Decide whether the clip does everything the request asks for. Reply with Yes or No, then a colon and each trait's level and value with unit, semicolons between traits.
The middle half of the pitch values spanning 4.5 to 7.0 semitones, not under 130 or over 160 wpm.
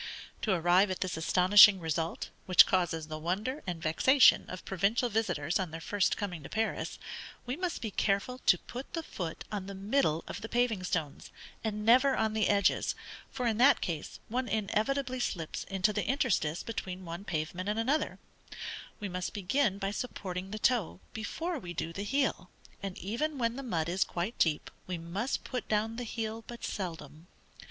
No: average, 4.8 semitones; average, 180 wpm